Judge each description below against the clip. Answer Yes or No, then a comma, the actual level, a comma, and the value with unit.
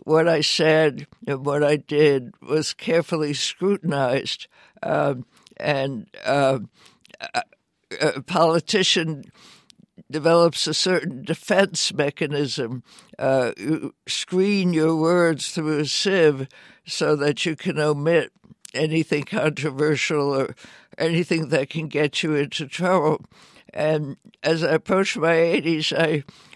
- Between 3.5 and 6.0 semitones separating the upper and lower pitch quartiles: No, narrow, 2.6 semitones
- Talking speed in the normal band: No, slow, 115 wpm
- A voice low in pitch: No, medium, 155 Hz